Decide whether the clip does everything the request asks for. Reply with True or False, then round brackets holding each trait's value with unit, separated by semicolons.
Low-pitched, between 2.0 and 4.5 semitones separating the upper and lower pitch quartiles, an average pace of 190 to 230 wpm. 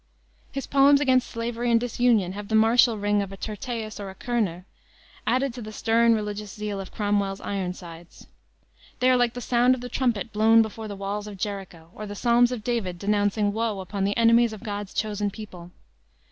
False (215 Hz; 2.9 semitones; 195 wpm)